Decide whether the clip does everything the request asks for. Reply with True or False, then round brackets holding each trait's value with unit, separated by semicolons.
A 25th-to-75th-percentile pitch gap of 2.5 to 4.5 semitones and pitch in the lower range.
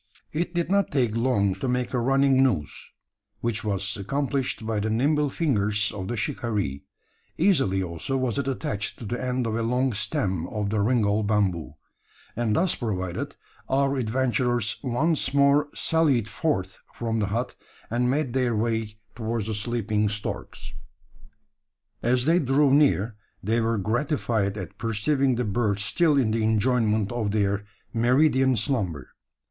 True (4.1 semitones; 115 Hz)